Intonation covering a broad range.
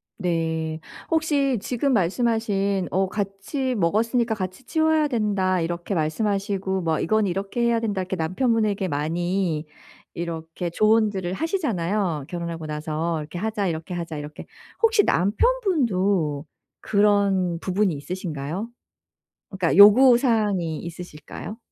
No: average, 4.7 semitones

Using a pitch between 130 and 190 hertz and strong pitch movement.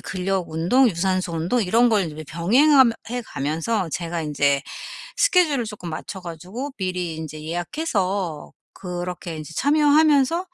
Yes: medium, 185 Hz; wide, 7.0 semitones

